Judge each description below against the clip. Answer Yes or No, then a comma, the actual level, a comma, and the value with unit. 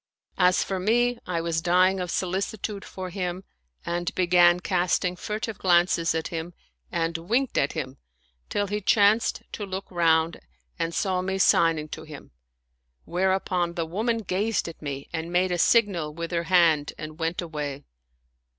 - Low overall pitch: No, medium, 175 Hz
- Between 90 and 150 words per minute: No, average, 160 wpm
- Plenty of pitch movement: No, narrow, 2.5 semitones